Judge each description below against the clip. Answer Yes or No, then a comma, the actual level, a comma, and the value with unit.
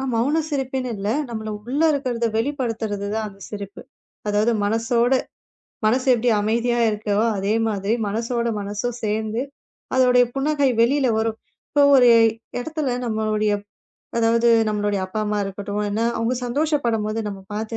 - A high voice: Yes, high, 225 Hz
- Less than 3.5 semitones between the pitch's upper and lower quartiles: Yes, average, 3.0 semitones